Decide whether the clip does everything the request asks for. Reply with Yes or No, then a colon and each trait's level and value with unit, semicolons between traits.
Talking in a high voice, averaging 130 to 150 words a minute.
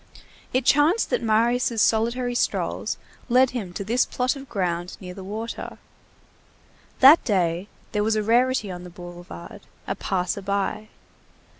Yes: high, 215 Hz; average, 145 wpm